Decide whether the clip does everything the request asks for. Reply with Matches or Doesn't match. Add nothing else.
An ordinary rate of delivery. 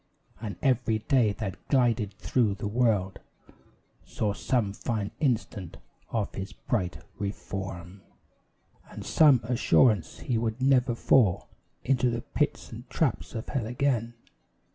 Doesn't match